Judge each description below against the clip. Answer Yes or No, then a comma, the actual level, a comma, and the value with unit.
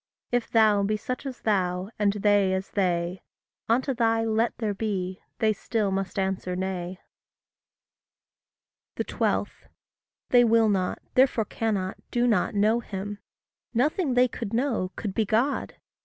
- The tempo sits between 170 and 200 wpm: No, average, 140 wpm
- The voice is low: No, high, 210 Hz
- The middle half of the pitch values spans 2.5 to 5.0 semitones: Yes, average, 3.3 semitones